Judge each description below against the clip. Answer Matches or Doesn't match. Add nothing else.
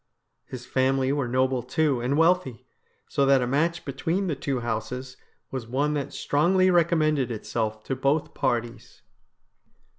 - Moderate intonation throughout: Matches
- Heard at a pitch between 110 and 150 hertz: Matches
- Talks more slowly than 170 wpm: Matches